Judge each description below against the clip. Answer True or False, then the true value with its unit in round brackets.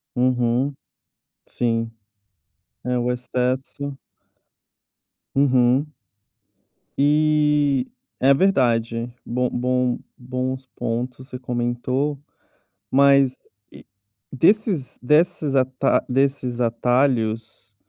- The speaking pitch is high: False (130 Hz)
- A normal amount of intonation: False (2.3 semitones)